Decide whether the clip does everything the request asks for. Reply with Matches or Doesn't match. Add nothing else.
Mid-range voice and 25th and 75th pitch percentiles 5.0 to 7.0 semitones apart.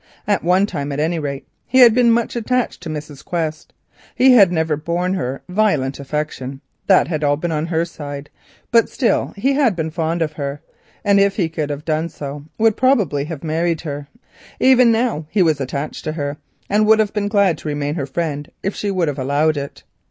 Matches